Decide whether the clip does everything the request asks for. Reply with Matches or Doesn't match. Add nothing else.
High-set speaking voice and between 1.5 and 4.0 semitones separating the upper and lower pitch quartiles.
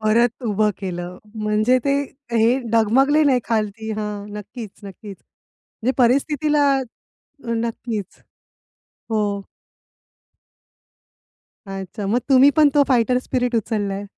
Matches